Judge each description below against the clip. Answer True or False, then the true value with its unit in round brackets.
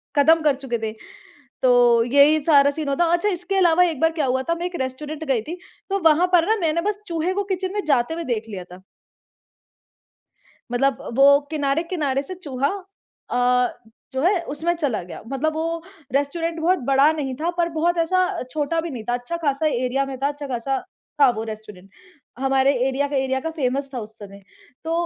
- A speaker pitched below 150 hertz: False (290 Hz)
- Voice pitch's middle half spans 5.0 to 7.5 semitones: False (4.1 semitones)